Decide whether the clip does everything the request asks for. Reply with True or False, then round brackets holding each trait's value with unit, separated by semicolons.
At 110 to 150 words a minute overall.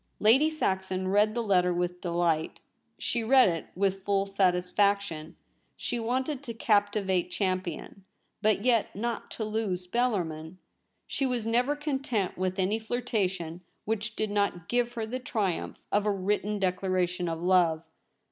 True (145 wpm)